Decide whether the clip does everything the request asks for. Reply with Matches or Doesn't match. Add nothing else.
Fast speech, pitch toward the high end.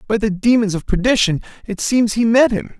Matches